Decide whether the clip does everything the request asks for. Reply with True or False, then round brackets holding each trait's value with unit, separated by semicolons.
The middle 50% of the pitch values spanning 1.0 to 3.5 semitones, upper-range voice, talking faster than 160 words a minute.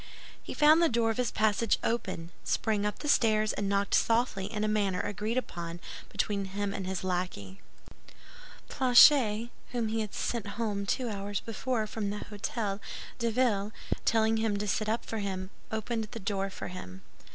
True (2.5 semitones; 210 Hz; 175 wpm)